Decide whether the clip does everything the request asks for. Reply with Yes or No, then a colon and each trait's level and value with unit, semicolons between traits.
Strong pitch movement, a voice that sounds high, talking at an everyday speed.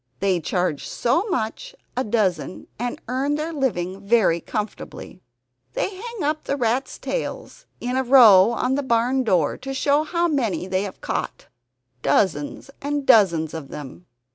Yes: wide, 7.2 semitones; high, 235 Hz; average, 155 wpm